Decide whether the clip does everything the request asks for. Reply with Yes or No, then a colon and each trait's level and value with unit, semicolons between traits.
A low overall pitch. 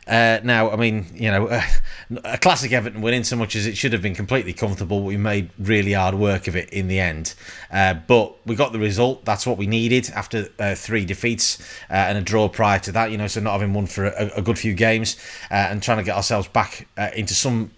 Yes: low, 105 Hz